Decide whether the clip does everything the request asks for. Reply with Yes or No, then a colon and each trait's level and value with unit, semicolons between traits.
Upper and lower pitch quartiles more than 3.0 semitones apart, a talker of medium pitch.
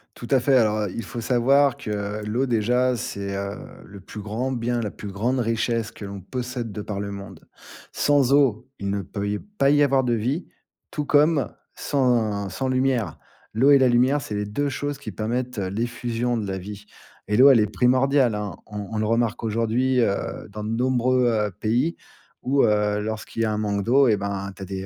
No: average, 3.7 semitones; low, 115 Hz